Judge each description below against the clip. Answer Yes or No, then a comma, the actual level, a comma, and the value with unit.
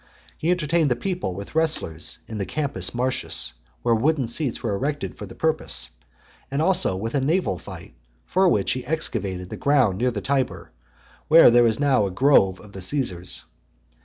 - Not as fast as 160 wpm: No, average, 180 wpm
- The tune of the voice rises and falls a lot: Yes, wide, 7.4 semitones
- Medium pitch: No, low, 125 Hz